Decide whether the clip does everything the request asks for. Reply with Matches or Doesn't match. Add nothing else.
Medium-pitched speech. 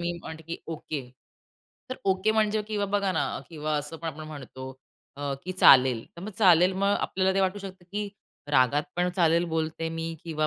Matches